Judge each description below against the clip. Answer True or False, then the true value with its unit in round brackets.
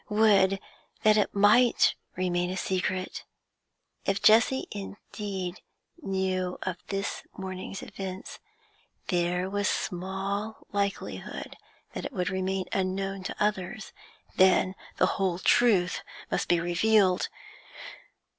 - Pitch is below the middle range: False (190 Hz)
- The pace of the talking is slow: True (110 wpm)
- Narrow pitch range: True (1.8 semitones)